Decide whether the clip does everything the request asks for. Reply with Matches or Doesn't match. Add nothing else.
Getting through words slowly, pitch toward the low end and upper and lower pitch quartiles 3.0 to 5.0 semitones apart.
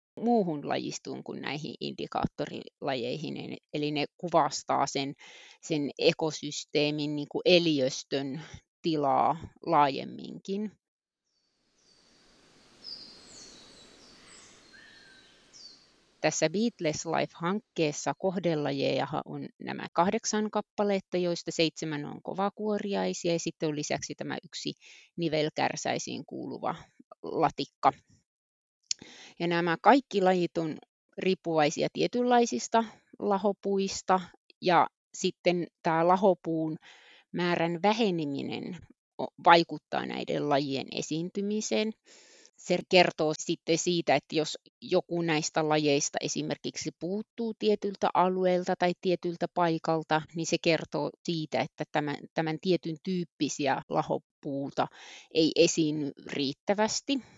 Doesn't match